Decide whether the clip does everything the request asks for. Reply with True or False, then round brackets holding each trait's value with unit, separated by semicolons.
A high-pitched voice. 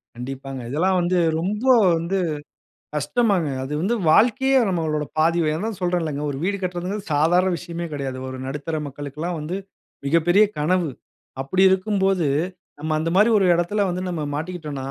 False (170 Hz)